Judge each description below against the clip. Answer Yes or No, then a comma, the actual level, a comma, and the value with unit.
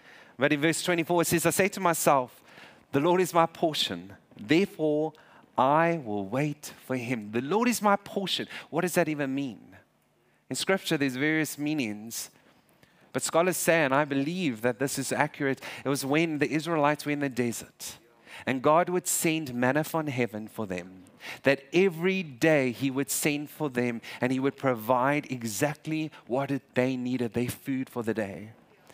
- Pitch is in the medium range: Yes, medium, 145 Hz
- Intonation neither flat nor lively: Yes, average, 4.3 semitones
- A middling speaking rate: Yes, average, 175 wpm